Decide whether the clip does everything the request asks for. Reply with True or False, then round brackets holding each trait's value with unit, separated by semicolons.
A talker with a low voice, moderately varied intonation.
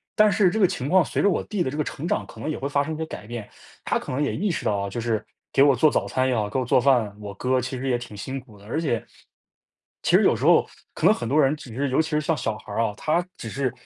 True (130 Hz; 4.8 semitones)